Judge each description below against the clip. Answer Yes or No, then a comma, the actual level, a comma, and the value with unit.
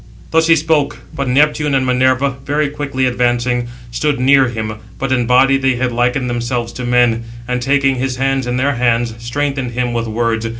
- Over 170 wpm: Yes, average, 185 wpm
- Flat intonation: Yes, narrow, 2.2 semitones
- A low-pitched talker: Yes, low, 125 Hz